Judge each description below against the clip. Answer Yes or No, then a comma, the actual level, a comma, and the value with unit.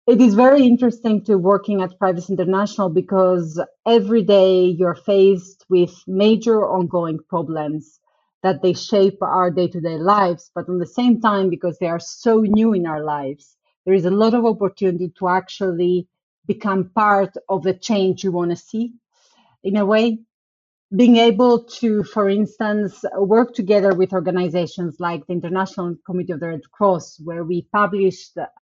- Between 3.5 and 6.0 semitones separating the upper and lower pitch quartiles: No, average, 2.9 semitones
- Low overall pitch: No, high, 190 Hz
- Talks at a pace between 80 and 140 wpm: No, average, 165 wpm